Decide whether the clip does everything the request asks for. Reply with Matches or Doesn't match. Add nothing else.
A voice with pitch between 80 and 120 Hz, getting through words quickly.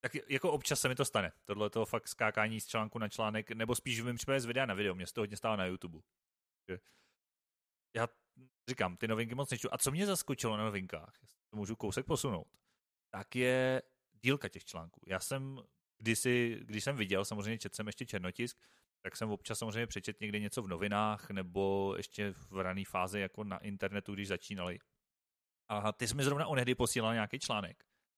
Matches